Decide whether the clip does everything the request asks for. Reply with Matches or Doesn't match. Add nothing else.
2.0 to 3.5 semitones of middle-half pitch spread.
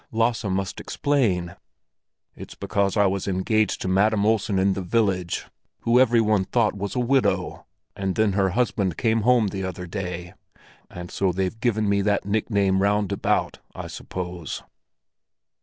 Matches